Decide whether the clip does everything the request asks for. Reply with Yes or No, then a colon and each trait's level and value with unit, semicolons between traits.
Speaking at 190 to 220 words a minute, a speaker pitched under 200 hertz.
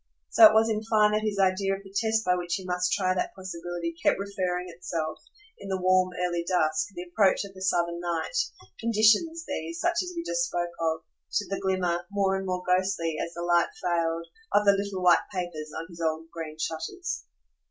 Yes: fast, 205 wpm; medium, 185 Hz